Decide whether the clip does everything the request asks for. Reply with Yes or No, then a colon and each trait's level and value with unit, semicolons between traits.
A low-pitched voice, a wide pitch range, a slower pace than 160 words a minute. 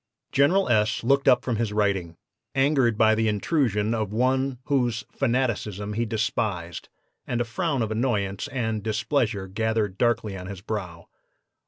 No: low, 110 Hz; average, 3.3 semitones; average, 150 wpm